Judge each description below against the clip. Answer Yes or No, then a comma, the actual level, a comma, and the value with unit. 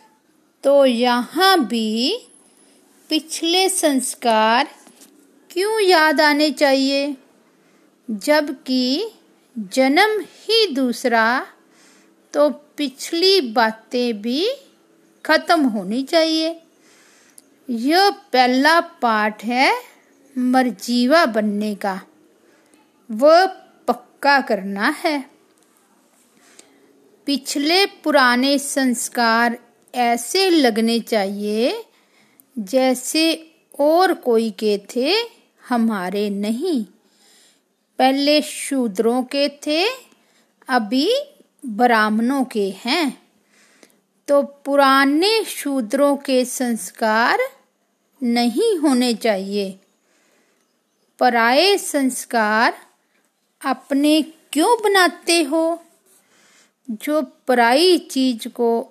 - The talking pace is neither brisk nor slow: No, slow, 70 wpm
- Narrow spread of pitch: No, average, 5.2 semitones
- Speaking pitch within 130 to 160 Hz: No, very high, 275 Hz